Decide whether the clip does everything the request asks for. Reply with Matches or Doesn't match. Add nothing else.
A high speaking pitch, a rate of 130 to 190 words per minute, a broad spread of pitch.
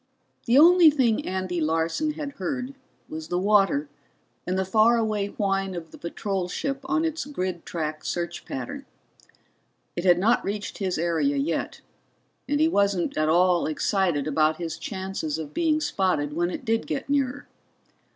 Matches